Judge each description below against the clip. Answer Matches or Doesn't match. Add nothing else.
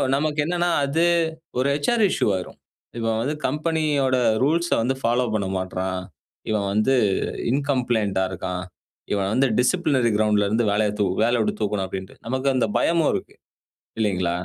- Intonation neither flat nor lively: Doesn't match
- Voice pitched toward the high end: Doesn't match